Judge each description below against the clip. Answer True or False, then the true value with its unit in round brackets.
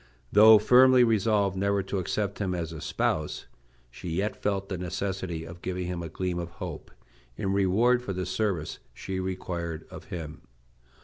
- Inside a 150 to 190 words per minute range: True (170 wpm)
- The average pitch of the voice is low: True (95 Hz)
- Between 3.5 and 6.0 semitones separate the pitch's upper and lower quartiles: False (2.7 semitones)